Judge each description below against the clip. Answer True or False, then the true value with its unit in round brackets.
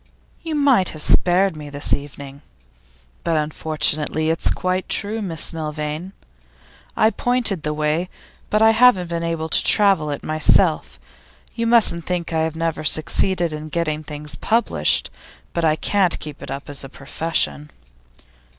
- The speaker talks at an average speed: True (150 wpm)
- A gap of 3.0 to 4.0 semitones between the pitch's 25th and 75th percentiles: True (3.7 semitones)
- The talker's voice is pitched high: False (160 Hz)